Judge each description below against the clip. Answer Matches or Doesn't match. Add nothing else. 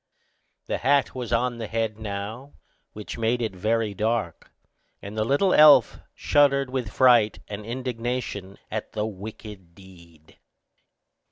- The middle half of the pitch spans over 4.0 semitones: Doesn't match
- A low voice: Matches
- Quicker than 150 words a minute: Doesn't match